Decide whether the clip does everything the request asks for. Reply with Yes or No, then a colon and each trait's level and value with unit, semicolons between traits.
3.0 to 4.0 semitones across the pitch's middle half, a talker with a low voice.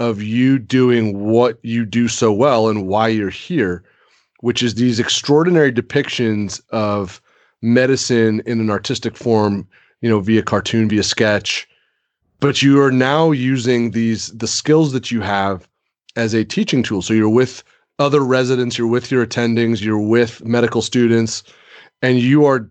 No: narrow, 2.6 semitones; low, 115 Hz